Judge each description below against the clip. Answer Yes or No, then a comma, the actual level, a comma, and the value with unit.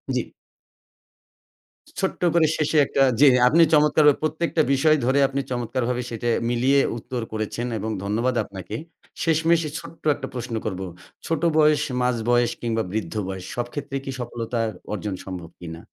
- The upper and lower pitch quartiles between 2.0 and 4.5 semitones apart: No, average, 5.3 semitones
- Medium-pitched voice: No, low, 125 Hz